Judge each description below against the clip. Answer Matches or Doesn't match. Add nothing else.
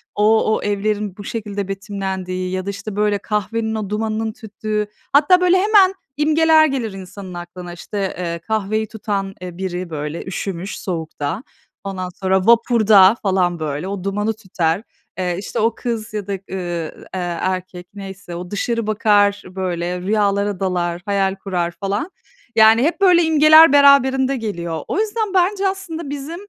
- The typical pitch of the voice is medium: Doesn't match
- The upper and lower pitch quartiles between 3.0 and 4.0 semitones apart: Matches